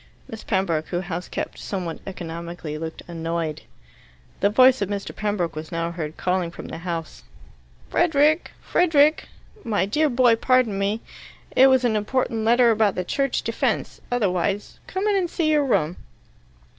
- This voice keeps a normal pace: Yes, average, 155 wpm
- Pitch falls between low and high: No, high, 205 Hz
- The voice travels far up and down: Yes, wide, 6.9 semitones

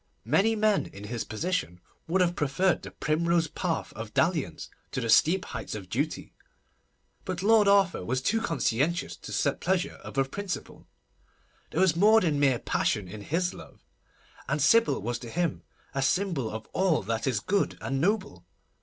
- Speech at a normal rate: Yes, average, 170 wpm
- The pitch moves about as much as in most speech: No, wide, 6.7 semitones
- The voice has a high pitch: No, medium, 165 Hz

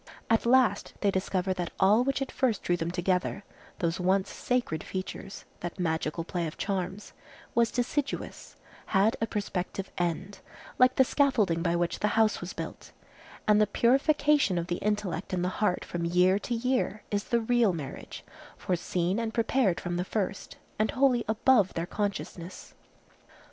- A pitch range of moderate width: Yes, average, 4.6 semitones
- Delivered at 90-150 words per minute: No, average, 160 wpm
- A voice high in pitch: Yes, high, 195 Hz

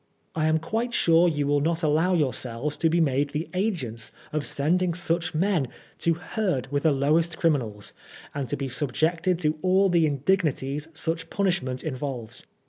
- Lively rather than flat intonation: No, average, 3.7 semitones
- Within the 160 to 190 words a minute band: Yes, average, 165 wpm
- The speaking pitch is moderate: Yes, medium, 155 Hz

